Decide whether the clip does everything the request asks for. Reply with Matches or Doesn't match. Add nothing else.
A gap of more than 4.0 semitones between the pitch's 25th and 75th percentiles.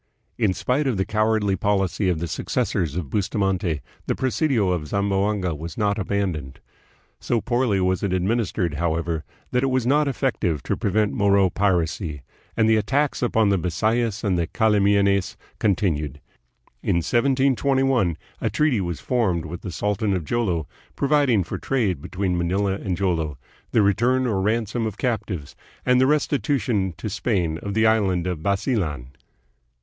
Matches